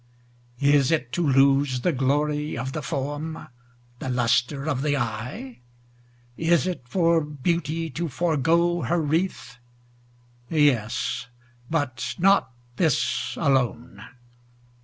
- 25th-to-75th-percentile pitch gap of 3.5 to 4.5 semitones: Yes, average, 4.2 semitones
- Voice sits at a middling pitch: Yes, medium, 145 Hz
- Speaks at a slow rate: Yes, slow, 110 wpm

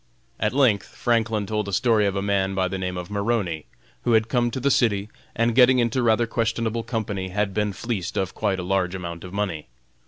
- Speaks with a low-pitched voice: Yes, low, 105 Hz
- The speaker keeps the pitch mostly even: No, average, 3.3 semitones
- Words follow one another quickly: Yes, fast, 215 wpm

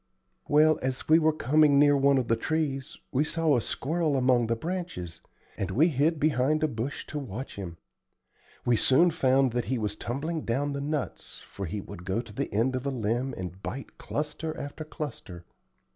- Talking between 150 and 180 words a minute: No, average, 190 wpm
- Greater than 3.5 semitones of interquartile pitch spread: Yes, average, 4.7 semitones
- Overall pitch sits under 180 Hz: Yes, low, 135 Hz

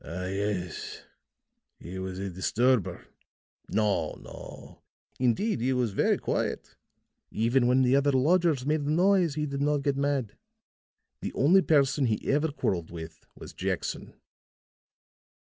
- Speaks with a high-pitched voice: No, low, 130 Hz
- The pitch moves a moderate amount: No, wide, 6.2 semitones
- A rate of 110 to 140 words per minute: Yes, slow, 135 wpm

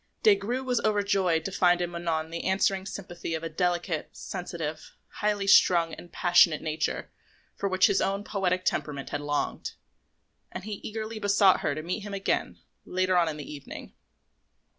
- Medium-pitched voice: Yes, medium, 180 Hz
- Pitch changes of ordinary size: Yes, average, 3.3 semitones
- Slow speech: No, average, 170 wpm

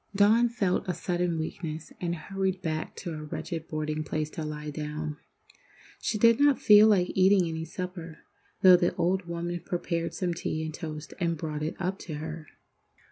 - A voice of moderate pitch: Yes, medium, 170 Hz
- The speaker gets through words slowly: No, average, 180 wpm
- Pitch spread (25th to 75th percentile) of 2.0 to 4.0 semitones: Yes, average, 3.1 semitones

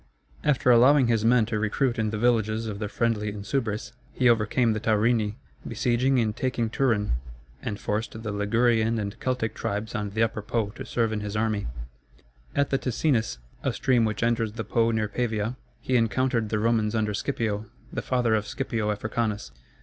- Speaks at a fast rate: No, average, 180 wpm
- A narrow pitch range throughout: Yes, narrow, 2.1 semitones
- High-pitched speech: No, low, 110 Hz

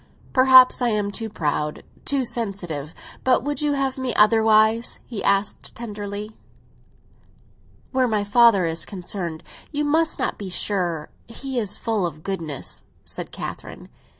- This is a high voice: Yes, high, 215 Hz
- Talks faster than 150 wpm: No, slow, 135 wpm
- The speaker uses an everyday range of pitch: Yes, average, 5.0 semitones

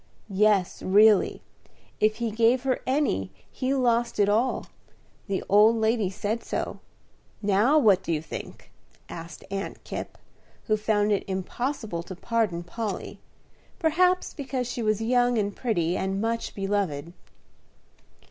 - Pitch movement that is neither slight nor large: Yes, average, 3.6 semitones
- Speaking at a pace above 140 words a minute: No, slow, 135 wpm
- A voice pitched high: Yes, high, 215 Hz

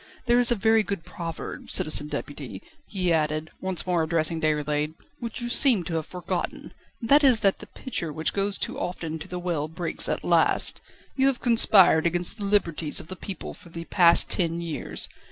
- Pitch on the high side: No, medium, 175 Hz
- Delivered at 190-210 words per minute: Yes, average, 195 wpm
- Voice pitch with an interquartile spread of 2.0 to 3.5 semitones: No, average, 4.4 semitones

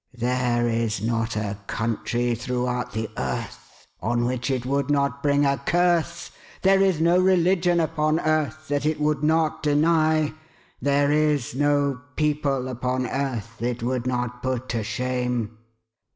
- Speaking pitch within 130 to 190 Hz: Yes, low, 135 Hz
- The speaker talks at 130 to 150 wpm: Yes, average, 145 wpm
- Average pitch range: Yes, average, 4.1 semitones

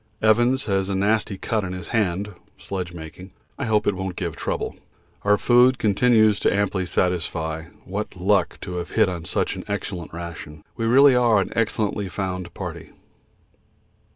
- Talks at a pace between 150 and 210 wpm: Yes, average, 165 wpm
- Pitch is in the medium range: No, low, 100 Hz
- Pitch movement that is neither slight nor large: Yes, average, 3.3 semitones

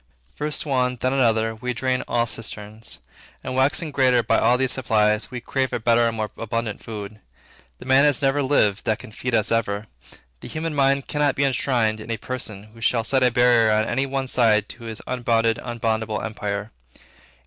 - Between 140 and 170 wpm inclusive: No, average, 190 wpm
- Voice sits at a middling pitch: No, low, 120 Hz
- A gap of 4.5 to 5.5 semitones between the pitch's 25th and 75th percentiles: No, average, 3.1 semitones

